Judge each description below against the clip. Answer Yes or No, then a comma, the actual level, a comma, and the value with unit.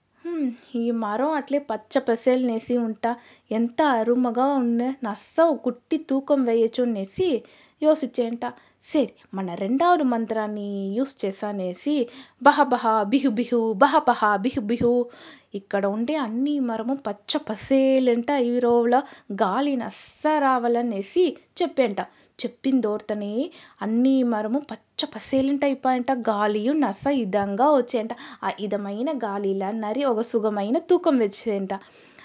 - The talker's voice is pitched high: Yes, high, 245 Hz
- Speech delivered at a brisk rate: No, average, 110 wpm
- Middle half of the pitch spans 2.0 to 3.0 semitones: No, average, 3.9 semitones